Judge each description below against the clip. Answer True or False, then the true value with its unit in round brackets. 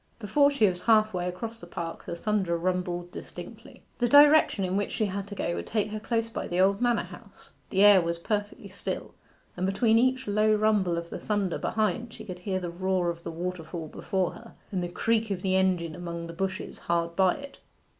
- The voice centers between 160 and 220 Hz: True (190 Hz)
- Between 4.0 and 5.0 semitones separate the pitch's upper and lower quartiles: False (3.6 semitones)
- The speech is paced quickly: True (215 wpm)